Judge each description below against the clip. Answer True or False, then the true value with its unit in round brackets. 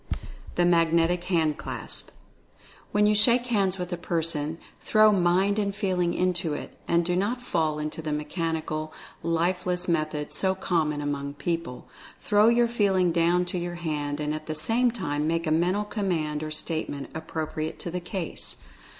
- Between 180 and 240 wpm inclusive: False (165 wpm)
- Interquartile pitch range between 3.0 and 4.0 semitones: True (3.5 semitones)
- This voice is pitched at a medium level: True (170 Hz)